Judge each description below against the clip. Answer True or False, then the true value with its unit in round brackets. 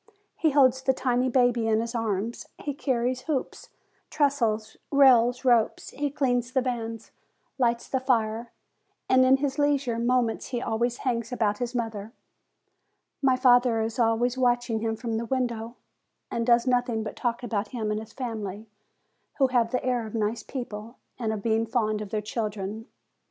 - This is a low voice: False (235 Hz)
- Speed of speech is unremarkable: True (165 wpm)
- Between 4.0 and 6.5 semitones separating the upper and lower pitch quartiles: False (2.4 semitones)